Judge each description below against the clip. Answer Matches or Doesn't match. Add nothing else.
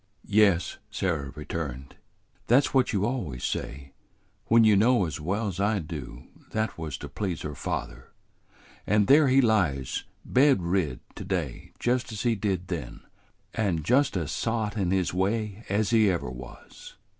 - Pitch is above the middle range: Doesn't match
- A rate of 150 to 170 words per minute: Matches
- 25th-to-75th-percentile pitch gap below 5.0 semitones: Doesn't match